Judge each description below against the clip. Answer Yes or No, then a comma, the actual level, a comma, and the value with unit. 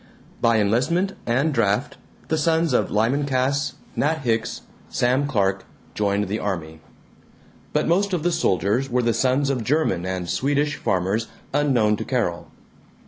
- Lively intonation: Yes, wide, 5.7 semitones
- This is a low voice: Yes, low, 125 Hz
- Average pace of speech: Yes, average, 145 wpm